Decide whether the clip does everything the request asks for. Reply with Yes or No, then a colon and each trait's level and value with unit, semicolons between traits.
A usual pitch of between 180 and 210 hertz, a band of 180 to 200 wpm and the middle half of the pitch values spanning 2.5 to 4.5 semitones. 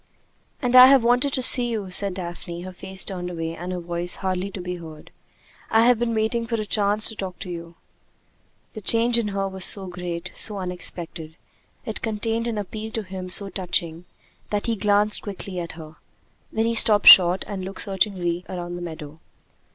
Yes: high, 190 Hz; average, 195 wpm; average, 3.7 semitones